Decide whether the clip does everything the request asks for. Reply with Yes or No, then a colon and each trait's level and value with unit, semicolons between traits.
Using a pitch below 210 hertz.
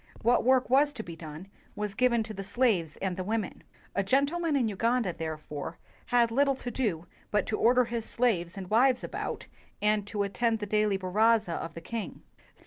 No: high, 215 Hz